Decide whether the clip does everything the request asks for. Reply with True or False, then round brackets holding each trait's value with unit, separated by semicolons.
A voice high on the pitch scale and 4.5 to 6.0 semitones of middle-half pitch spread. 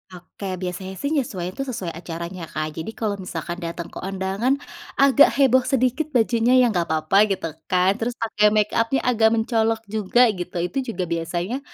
True (205 Hz; 5.0 semitones)